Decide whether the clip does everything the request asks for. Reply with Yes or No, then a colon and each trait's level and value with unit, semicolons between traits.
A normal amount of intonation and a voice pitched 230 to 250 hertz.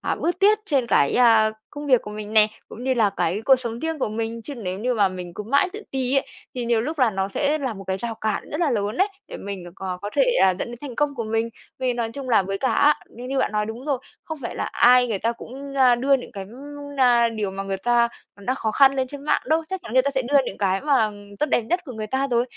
Yes: average, 4.4 semitones; high, 240 Hz